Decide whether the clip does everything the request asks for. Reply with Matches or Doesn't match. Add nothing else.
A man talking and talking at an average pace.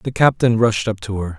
Doesn't match